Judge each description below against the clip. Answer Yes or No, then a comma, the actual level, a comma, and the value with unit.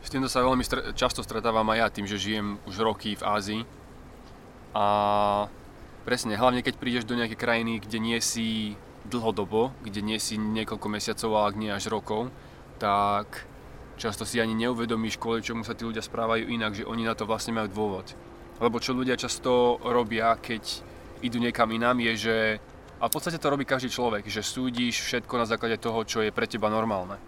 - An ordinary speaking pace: No, fast, 185 wpm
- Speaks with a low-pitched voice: Yes, low, 115 Hz